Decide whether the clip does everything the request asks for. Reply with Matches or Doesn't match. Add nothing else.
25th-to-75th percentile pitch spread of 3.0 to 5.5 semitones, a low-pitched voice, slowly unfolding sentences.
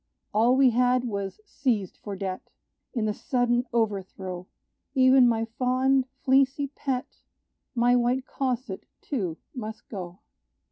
Doesn't match